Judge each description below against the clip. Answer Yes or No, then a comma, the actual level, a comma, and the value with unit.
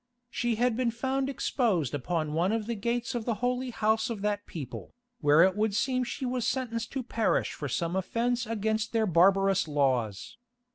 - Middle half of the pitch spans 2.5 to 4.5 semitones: No, average, 5.0 semitones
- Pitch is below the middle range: No, high, 220 Hz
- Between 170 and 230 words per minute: Yes, average, 185 wpm